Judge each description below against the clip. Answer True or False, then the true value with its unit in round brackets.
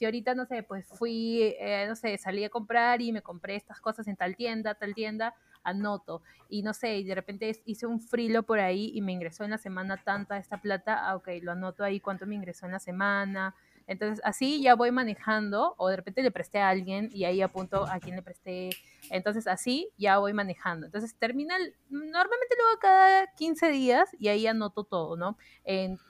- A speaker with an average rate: False (210 wpm)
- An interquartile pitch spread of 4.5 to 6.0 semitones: False (3.3 semitones)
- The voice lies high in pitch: True (210 Hz)